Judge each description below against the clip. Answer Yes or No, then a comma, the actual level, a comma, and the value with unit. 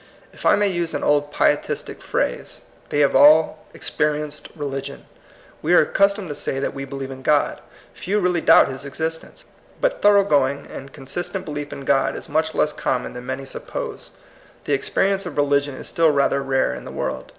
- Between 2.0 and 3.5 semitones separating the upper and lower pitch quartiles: Yes, average, 3.2 semitones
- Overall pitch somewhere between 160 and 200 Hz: No, medium, 145 Hz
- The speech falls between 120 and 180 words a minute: No, average, 195 wpm